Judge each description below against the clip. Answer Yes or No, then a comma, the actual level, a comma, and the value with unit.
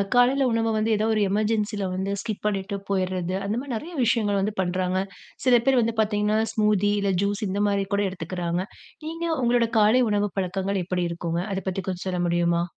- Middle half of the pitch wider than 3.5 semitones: No, average, 2.9 semitones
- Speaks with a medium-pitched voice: No, high, 205 Hz